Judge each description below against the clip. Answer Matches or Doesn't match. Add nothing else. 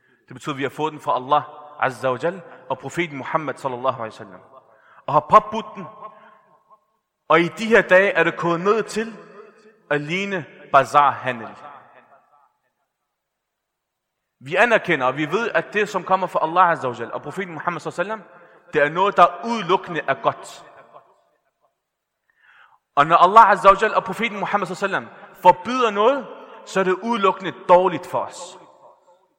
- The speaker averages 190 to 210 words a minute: Doesn't match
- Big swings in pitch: Matches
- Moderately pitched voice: Matches